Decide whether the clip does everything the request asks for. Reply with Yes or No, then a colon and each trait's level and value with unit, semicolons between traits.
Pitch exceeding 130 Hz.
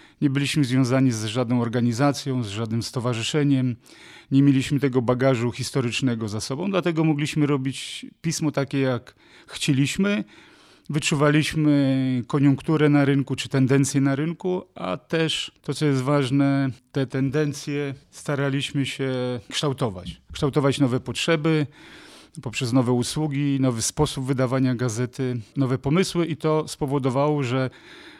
Yes: medium, 140 Hz